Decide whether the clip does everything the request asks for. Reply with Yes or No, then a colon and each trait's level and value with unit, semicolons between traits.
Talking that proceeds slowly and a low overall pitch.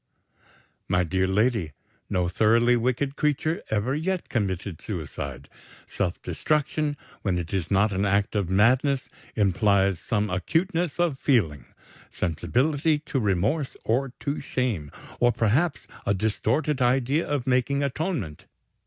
Yes: slow, 125 wpm; low, 115 Hz